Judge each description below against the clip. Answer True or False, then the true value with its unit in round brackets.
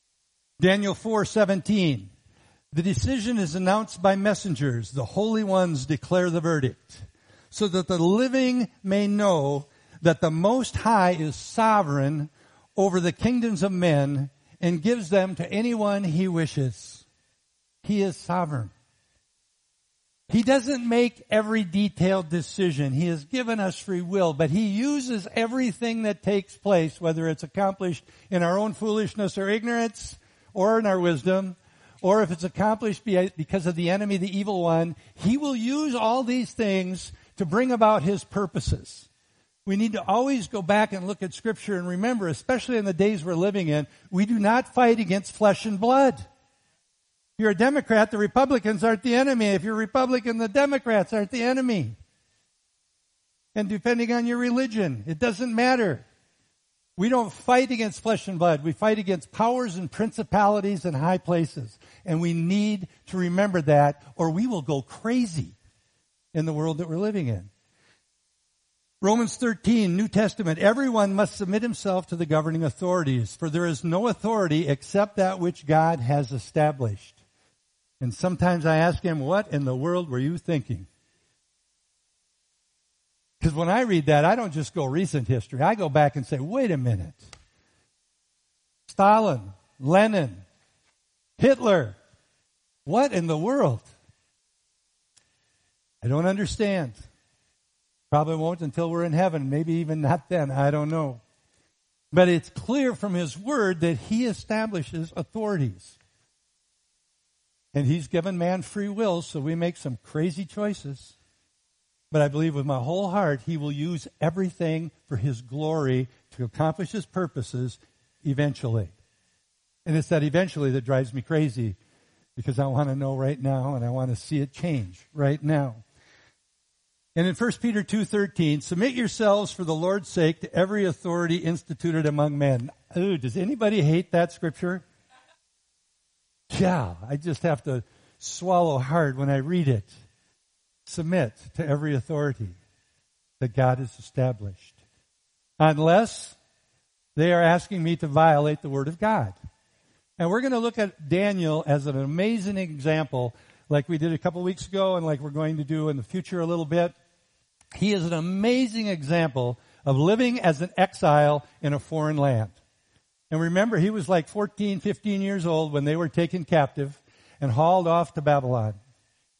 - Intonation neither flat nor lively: False (6.4 semitones)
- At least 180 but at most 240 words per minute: False (155 wpm)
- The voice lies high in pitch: False (170 Hz)